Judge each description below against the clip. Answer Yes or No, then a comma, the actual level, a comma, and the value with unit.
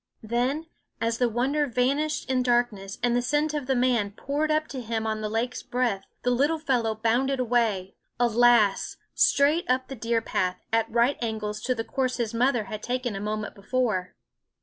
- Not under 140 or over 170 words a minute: No, average, 185 wpm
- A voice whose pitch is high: Yes, high, 240 Hz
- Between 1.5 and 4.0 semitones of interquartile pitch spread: Yes, average, 2.9 semitones